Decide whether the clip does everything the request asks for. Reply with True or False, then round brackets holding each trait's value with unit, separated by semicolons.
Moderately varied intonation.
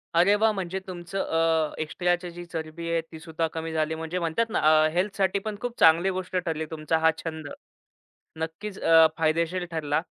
False (2.3 semitones)